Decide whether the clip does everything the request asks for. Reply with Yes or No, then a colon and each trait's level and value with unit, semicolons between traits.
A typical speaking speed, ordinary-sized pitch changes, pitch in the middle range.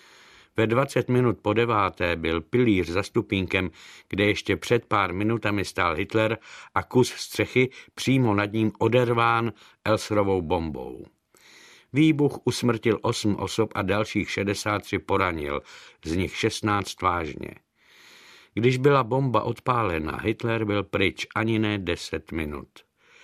No: average, 125 wpm; average, 3.0 semitones; low, 105 Hz